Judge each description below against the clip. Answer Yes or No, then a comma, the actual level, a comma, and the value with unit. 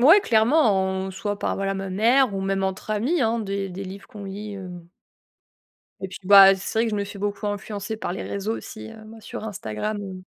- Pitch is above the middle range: Yes, high, 200 Hz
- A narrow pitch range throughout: Yes, narrow, 2.2 semitones